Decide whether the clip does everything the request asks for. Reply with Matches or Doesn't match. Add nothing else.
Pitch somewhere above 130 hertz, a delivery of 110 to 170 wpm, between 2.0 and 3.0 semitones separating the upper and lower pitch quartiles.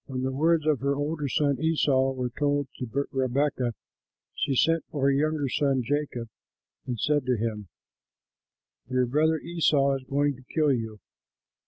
Matches